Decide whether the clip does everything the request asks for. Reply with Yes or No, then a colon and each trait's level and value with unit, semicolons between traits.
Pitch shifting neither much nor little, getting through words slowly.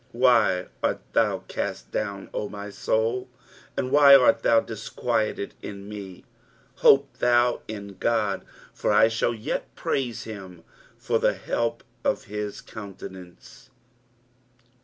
Yes: average, 3.2 semitones; slow, 130 wpm